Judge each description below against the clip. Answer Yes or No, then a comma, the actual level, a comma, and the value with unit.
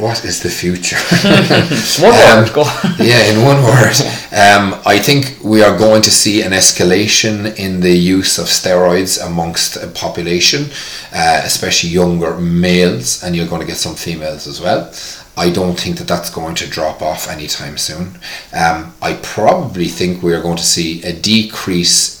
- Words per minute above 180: No, average, 170 wpm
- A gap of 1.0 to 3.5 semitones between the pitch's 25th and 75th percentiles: No, average, 3.9 semitones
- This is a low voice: Yes, very low, 90 Hz